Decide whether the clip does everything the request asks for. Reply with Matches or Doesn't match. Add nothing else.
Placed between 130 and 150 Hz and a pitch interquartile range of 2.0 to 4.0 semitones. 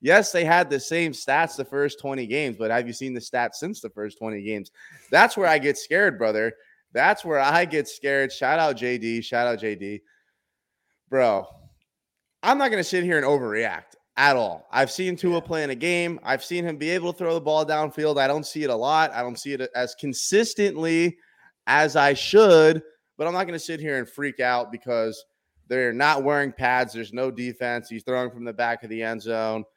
Doesn't match